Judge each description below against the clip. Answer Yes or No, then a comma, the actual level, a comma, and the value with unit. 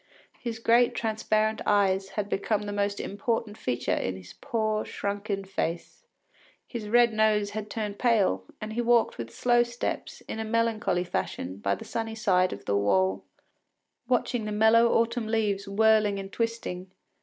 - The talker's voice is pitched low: No, high, 215 Hz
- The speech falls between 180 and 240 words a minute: No, average, 160 wpm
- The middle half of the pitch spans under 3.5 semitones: Yes, average, 2.8 semitones